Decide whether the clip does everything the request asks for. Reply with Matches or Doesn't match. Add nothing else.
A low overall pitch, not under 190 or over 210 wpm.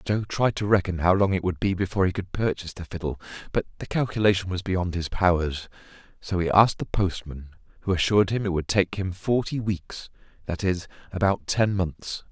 Matches